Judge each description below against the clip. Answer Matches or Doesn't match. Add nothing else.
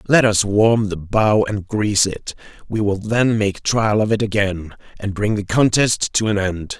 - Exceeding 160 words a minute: Matches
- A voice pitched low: Matches